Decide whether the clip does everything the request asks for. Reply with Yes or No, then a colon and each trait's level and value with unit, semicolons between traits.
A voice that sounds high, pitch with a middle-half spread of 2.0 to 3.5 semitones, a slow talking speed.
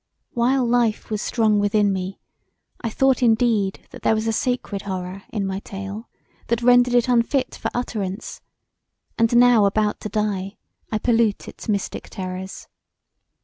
No: high, 215 Hz; average, 3.2 semitones; average, 150 wpm